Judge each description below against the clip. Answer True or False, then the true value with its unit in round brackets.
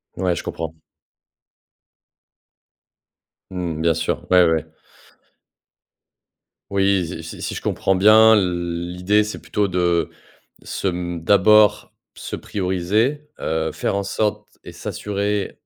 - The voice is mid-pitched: False (90 Hz)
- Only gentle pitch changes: False (3.1 semitones)